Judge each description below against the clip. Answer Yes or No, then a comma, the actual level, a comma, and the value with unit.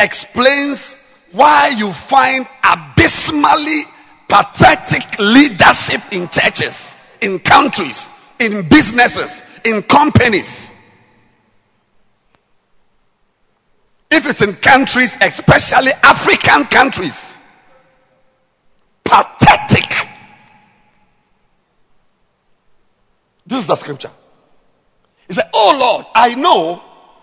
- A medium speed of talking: No, slow, 75 wpm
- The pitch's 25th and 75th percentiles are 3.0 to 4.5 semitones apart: Yes, average, 4.2 semitones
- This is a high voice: Yes, very high, 260 Hz